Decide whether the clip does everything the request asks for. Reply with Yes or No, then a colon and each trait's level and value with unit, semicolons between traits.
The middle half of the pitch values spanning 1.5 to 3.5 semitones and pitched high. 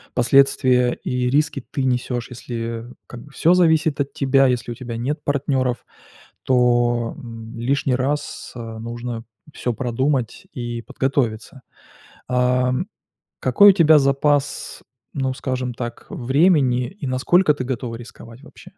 No: narrow, 2.6 semitones; low, 125 Hz